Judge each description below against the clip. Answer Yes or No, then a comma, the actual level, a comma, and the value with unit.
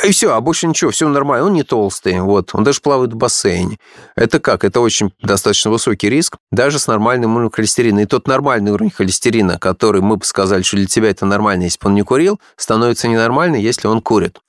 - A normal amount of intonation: Yes, average, 4.8 semitones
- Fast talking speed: Yes, fast, 215 wpm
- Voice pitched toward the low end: Yes, low, 110 Hz